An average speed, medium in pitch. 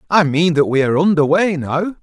No: fast, 210 wpm; medium, 165 Hz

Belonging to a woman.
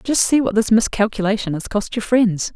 Yes: female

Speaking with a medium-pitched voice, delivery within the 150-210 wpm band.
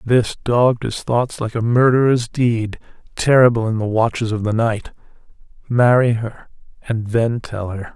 No: low, 115 Hz; average, 160 wpm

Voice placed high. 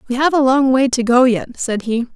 Yes: very high, 250 Hz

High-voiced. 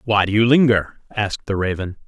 No: low, 105 Hz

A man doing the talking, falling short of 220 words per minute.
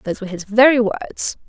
No: female; fast, 205 wpm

